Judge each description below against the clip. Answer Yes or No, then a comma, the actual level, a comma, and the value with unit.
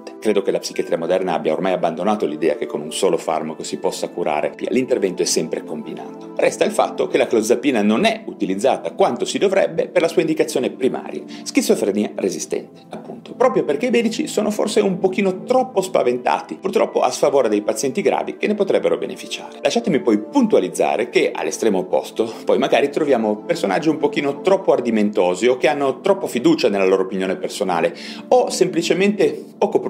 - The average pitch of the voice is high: Yes, high, 195 Hz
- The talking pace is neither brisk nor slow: No, fast, 175 wpm